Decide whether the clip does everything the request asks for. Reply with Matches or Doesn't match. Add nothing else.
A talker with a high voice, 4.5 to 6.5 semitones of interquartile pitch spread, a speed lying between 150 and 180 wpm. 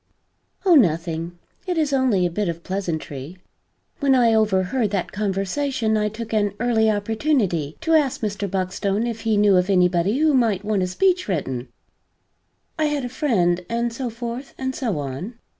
Matches